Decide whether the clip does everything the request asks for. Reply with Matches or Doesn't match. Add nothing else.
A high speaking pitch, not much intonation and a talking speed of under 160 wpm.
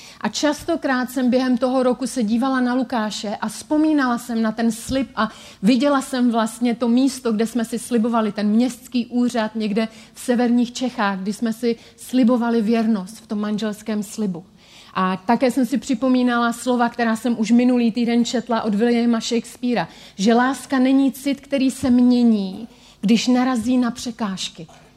Doesn't match